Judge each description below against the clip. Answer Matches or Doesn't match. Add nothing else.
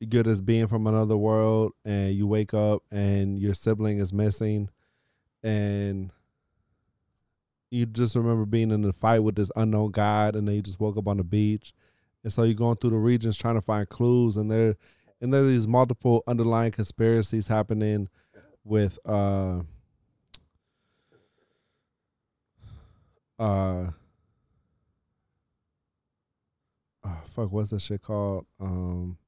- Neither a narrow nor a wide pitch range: Doesn't match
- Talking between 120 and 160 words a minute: Matches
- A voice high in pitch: Doesn't match